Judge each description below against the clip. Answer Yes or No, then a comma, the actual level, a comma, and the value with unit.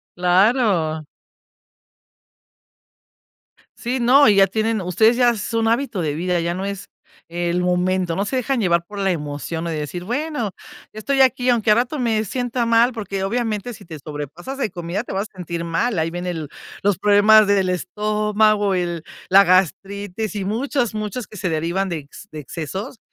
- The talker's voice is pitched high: Yes, high, 200 Hz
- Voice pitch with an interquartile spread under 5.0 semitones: Yes, average, 4.4 semitones